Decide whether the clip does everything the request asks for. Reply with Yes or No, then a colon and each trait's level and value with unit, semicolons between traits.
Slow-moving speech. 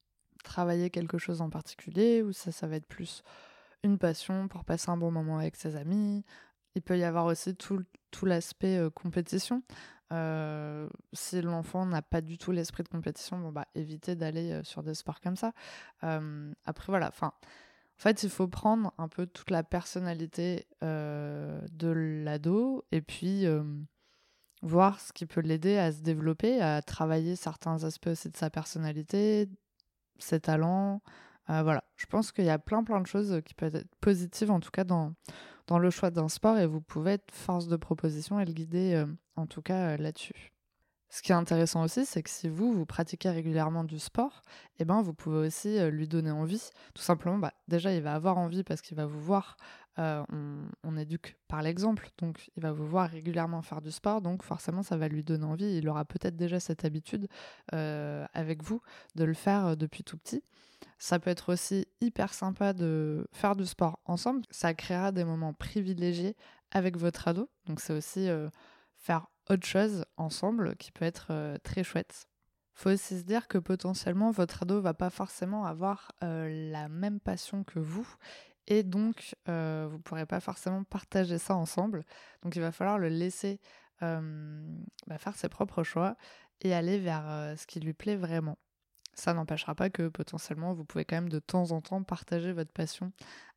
No: average, 190 wpm